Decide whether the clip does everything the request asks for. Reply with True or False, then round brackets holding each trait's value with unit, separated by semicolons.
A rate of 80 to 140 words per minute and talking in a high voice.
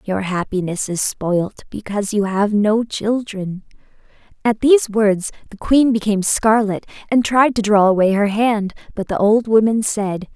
False (160 wpm; 210 Hz)